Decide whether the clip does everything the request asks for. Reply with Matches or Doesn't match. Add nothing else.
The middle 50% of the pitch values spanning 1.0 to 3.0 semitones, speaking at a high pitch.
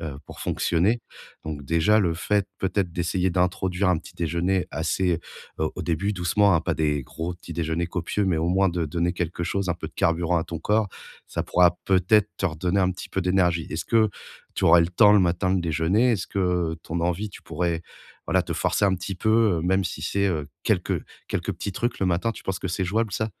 Doesn't match